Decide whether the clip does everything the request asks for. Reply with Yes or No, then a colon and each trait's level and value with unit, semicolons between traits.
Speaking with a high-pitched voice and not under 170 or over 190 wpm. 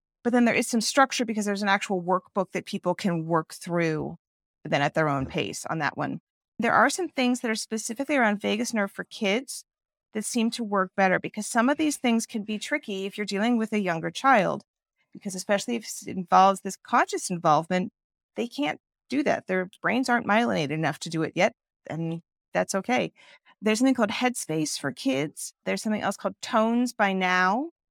No: high, 210 Hz; average, 200 wpm